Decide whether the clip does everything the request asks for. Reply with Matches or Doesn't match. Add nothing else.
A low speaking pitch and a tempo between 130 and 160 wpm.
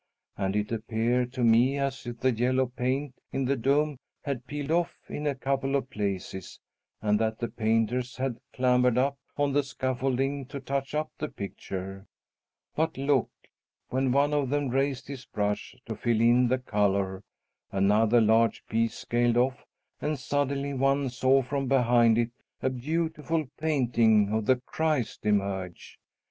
Matches